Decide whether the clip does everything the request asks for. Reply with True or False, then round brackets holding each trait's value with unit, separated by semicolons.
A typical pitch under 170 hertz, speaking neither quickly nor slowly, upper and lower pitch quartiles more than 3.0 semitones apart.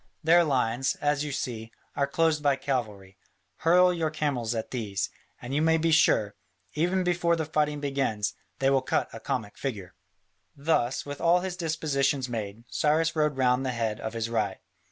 True (140 Hz; 175 wpm; 5.3 semitones)